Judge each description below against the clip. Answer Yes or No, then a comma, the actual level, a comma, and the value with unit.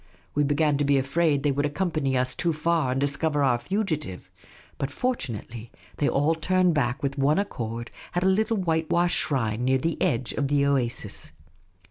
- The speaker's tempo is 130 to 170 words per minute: No, average, 185 wpm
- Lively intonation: No, average, 3.9 semitones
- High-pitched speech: No, medium, 145 Hz